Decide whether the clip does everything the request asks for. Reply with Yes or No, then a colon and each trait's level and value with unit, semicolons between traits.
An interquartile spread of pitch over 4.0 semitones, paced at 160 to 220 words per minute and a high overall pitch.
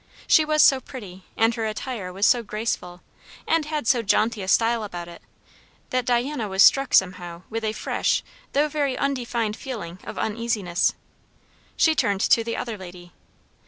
Yes: average, 4.9 semitones; average, 165 wpm; high, 225 Hz